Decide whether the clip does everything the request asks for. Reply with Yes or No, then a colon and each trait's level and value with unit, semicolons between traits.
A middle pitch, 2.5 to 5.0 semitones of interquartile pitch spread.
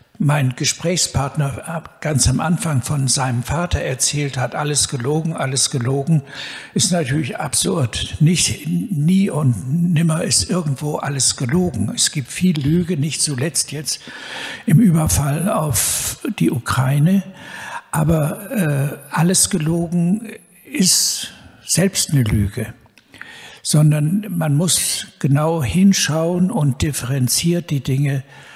Yes: medium, 150 Hz; average, 4.3 semitones